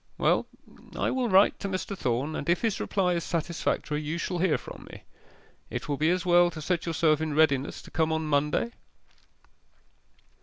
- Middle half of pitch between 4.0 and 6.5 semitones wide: No, average, 2.9 semitones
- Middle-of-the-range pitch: Yes, medium, 165 Hz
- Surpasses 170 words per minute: Yes, average, 185 wpm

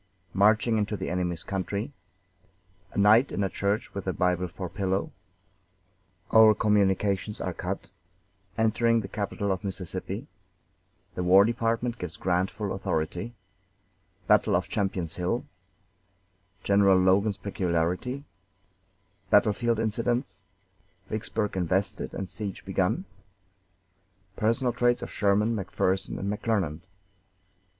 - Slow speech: Yes, slow, 115 wpm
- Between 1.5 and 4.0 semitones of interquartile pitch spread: Yes, average, 2.8 semitones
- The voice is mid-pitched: No, low, 100 Hz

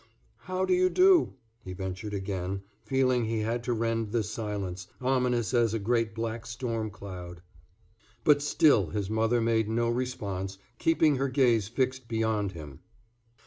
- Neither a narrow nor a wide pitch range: Yes, average, 3.9 semitones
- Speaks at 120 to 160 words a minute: Yes, average, 150 wpm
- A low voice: Yes, low, 115 Hz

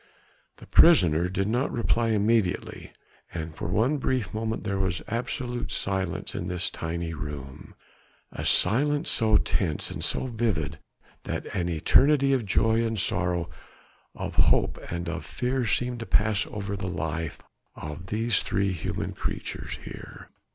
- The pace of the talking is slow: No, average, 145 wpm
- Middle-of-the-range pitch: No, low, 100 Hz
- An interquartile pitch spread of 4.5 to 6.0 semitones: Yes, average, 5.2 semitones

